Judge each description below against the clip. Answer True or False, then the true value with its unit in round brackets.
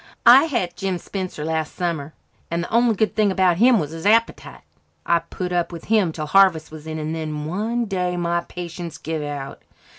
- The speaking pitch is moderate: True (175 Hz)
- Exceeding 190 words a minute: True (200 wpm)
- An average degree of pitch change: True (3.9 semitones)